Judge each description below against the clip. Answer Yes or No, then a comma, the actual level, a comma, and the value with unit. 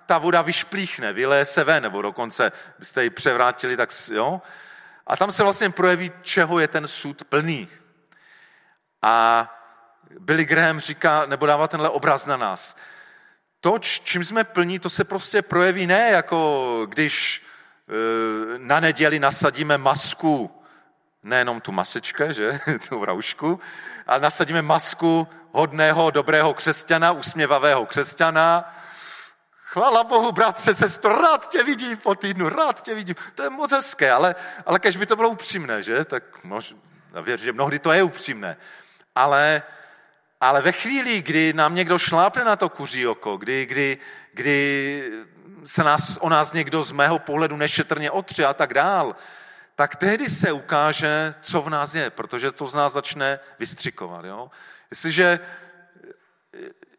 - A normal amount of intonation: Yes, average, 4.0 semitones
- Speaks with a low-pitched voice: No, medium, 160 Hz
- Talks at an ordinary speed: Yes, average, 145 wpm